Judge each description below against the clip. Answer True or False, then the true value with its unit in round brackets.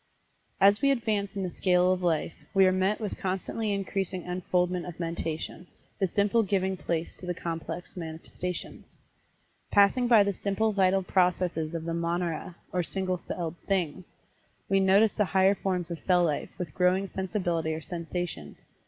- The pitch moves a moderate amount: False (2.3 semitones)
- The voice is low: False (185 Hz)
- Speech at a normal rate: True (160 wpm)